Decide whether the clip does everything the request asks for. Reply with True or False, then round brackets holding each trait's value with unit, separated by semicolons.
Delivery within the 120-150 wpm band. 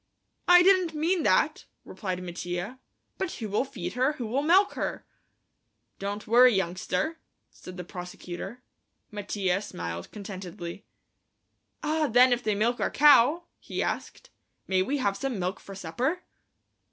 True (135 wpm)